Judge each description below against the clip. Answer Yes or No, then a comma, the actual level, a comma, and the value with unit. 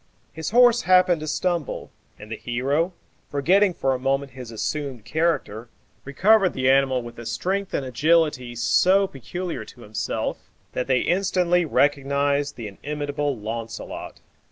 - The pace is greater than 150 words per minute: No, average, 140 wpm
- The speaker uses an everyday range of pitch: No, wide, 5.7 semitones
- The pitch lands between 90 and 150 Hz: Yes, medium, 140 Hz